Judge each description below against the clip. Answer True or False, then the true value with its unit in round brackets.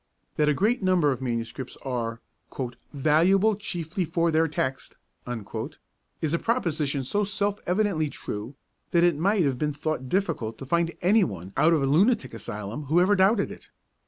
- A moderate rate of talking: True (165 wpm)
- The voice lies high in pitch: False (160 Hz)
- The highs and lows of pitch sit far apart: True (5.9 semitones)